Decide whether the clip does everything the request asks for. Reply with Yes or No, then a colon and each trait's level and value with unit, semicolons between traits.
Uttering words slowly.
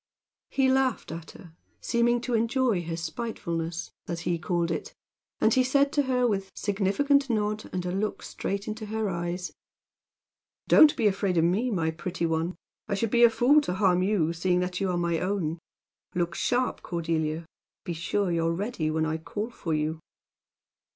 No: average, 180 wpm